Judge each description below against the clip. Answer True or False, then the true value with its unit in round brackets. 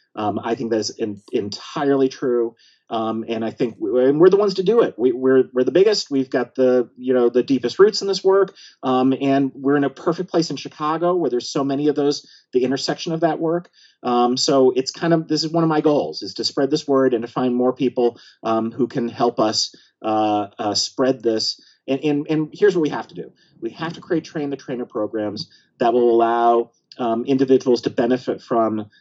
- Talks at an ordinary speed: False (225 wpm)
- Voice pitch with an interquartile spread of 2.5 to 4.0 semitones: False (4.4 semitones)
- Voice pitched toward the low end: True (130 Hz)